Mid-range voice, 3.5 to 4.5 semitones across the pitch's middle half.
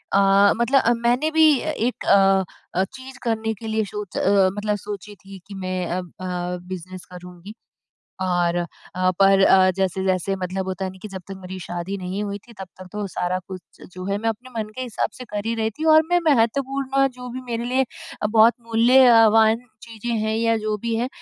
No: high, 205 Hz; average, 3.8 semitones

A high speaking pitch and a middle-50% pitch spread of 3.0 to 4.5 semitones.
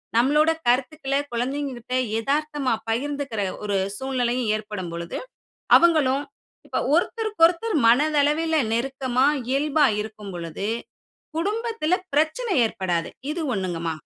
No: very high, 270 Hz; wide, 5.5 semitones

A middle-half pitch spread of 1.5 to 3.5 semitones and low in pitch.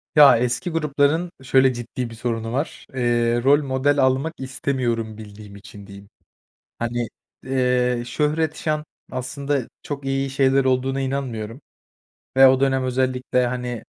Yes: narrow, 2.4 semitones; low, 130 Hz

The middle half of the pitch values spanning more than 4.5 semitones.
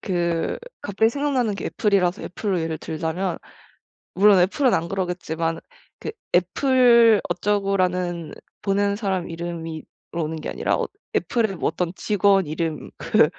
No: average, 3.5 semitones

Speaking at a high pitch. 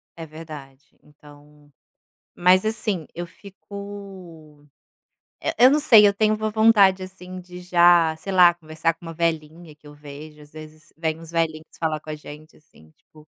No: medium, 165 Hz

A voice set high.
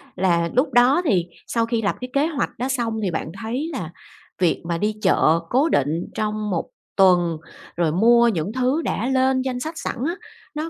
Yes: high, 230 Hz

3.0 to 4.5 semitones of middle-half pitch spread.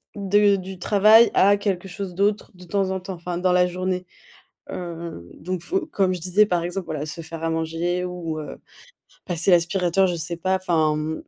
No: narrow, 2.4 semitones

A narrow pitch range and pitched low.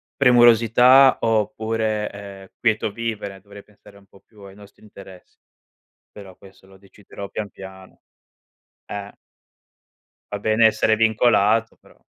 Yes: narrow, 2.1 semitones; low, 105 Hz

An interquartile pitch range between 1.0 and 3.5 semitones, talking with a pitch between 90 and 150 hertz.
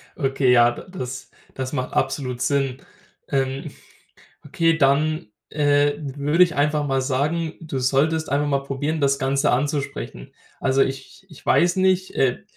Yes: narrow, 2.4 semitones; medium, 140 Hz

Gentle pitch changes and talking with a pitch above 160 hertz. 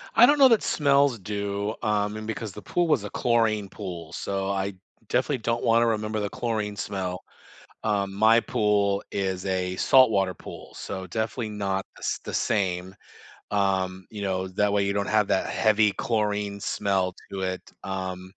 No: narrow, 2.3 semitones; low, 100 Hz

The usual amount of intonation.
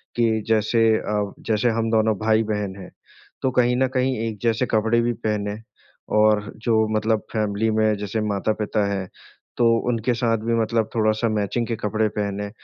No: narrow, 1.6 semitones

